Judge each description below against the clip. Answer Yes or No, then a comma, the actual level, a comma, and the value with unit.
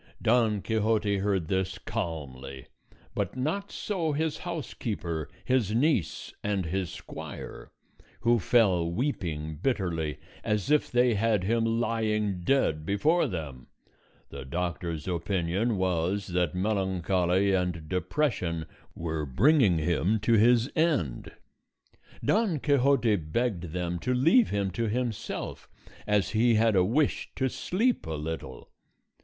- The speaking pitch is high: No, low, 100 Hz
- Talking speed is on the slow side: Yes, slow, 125 wpm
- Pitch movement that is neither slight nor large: No, wide, 5.9 semitones